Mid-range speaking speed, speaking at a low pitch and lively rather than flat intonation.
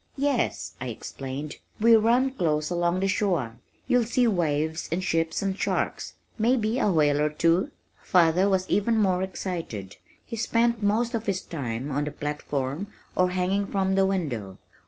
No: average, 165 wpm; medium, 185 Hz; wide, 5.9 semitones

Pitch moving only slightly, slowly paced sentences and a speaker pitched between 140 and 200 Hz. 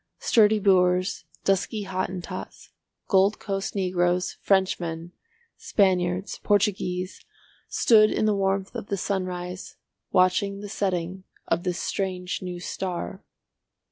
Yes: narrow, 1.6 semitones; slow, 110 wpm; high, 190 Hz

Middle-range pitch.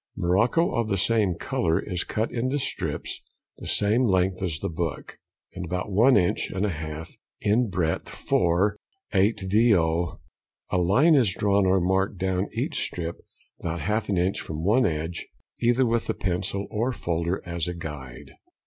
No: very low, 95 Hz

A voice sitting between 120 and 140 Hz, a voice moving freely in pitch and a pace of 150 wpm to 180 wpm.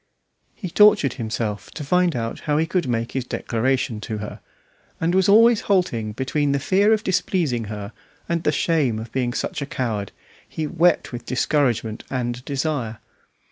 Yes: low, 135 Hz; wide, 6.4 semitones; average, 165 wpm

